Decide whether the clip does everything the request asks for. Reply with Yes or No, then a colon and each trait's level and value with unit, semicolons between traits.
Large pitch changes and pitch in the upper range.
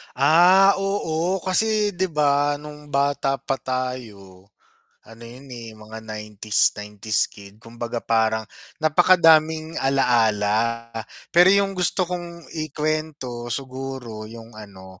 No: wide, 6.3 semitones; low, 135 Hz